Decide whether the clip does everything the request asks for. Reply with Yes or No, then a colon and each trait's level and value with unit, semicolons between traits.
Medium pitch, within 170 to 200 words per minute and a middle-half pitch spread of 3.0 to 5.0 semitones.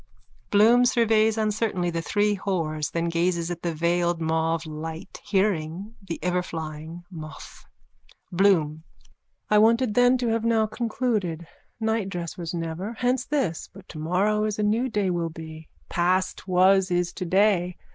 No: medium, 180 Hz; average, 145 wpm; average, 4.3 semitones